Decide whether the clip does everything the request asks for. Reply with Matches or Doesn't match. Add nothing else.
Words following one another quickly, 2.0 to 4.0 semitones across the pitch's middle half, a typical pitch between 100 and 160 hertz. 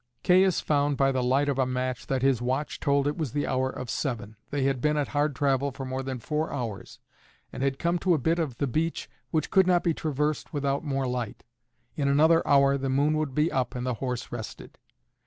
Matches